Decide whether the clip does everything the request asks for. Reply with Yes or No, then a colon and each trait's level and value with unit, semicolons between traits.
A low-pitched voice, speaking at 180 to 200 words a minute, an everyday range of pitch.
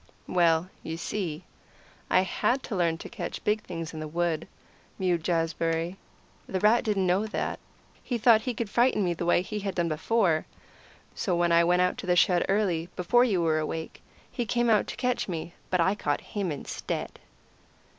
No: medium, 180 Hz; average, 190 wpm; average, 4.0 semitones